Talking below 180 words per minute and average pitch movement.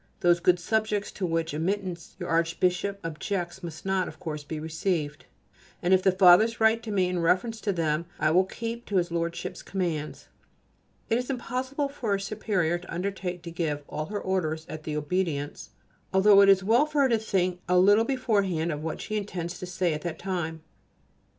No: average, 195 wpm; average, 3.6 semitones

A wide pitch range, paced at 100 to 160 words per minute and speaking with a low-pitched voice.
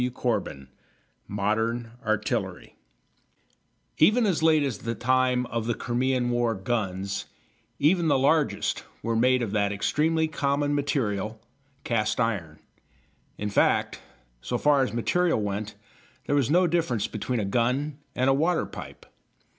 No: average, 5.0 semitones; average, 140 wpm; low, 125 Hz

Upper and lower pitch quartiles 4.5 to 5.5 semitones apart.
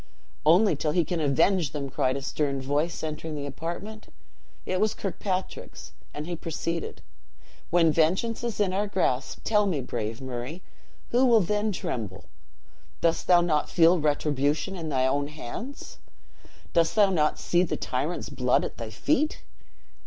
Yes: average, 4.9 semitones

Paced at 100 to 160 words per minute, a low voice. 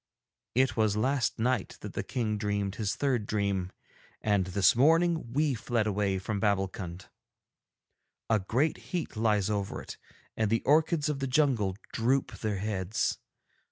Yes: average, 150 wpm; low, 110 Hz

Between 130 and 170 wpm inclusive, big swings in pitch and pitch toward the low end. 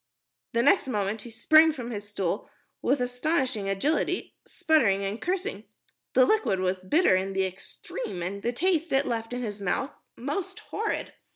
No: average, 160 wpm; wide, 7.9 semitones; high, 240 Hz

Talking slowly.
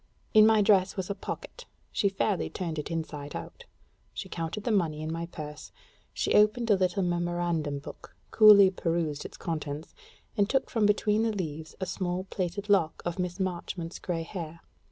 No: average, 175 wpm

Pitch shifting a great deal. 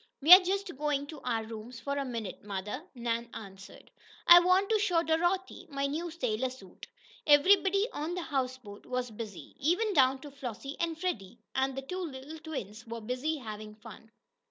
Yes: wide, 6.4 semitones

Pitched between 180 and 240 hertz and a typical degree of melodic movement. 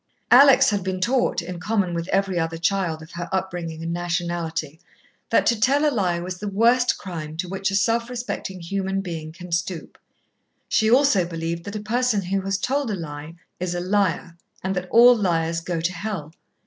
Yes: medium, 185 Hz; average, 3.7 semitones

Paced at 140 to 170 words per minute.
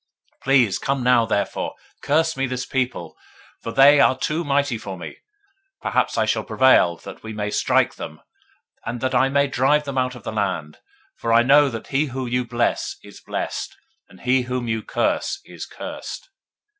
No: average, 185 wpm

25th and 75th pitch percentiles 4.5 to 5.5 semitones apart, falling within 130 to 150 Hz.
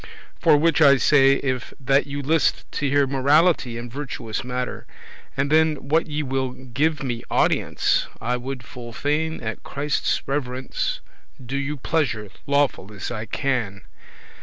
No: average, 3.0 semitones; low, 135 Hz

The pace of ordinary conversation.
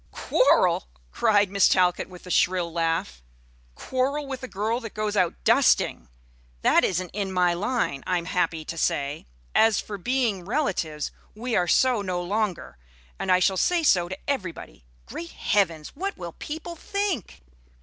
Yes: average, 160 wpm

